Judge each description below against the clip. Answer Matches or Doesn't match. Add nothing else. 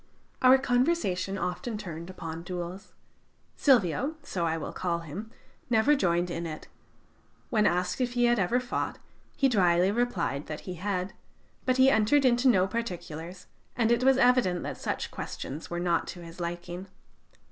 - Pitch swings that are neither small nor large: Doesn't match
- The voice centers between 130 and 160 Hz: Doesn't match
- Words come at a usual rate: Matches